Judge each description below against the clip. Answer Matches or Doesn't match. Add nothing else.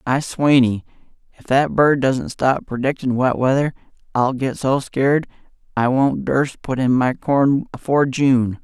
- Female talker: Doesn't match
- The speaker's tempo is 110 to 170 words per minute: Matches